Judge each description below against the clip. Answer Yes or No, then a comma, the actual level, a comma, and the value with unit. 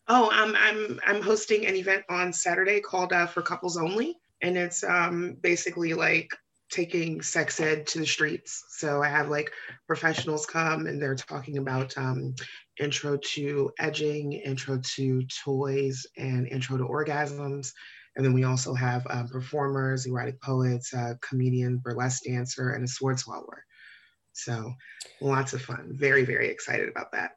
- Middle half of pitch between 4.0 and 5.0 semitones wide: Yes, average, 4.5 semitones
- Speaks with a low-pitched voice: No, medium, 145 Hz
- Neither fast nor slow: Yes, average, 160 wpm